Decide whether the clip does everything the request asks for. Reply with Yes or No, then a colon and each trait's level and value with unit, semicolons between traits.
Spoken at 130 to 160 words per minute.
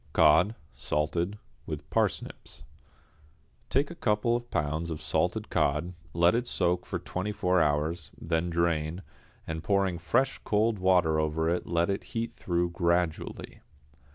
Yes: average, 140 wpm